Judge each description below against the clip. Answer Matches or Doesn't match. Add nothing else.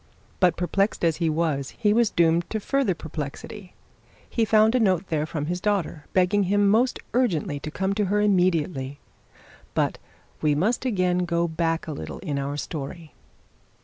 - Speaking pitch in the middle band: Matches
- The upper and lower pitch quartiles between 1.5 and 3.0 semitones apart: Doesn't match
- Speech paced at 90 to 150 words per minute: Doesn't match